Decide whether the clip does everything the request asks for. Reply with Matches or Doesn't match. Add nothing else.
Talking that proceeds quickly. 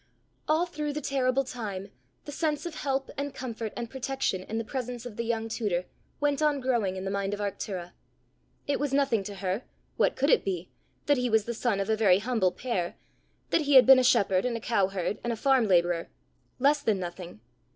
Matches